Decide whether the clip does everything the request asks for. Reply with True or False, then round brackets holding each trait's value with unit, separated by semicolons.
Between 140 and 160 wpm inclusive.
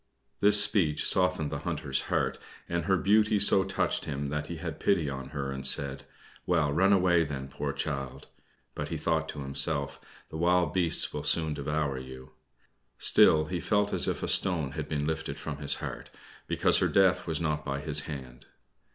False (185 wpm)